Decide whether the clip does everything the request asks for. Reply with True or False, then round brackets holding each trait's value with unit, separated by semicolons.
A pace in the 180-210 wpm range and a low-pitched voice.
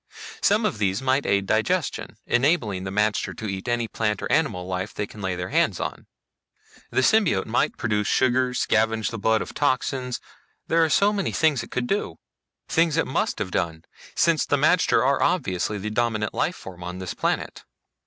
True (190 wpm; 110 Hz)